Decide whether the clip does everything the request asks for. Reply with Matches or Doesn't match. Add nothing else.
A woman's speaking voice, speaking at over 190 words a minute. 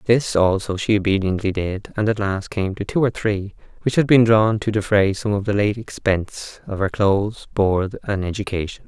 Doesn't match